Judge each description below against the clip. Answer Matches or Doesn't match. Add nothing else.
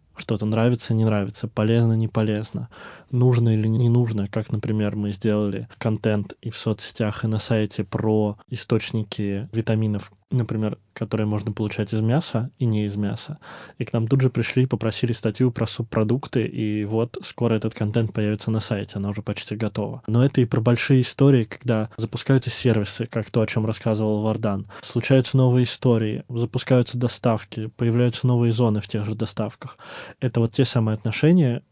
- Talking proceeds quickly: Matches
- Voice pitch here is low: Matches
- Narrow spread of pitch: Matches